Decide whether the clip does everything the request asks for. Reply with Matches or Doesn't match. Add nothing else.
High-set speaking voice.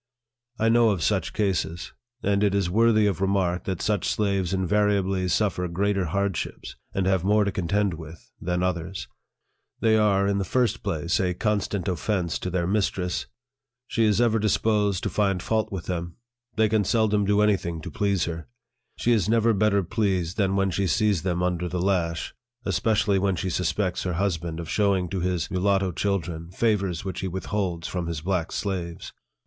Doesn't match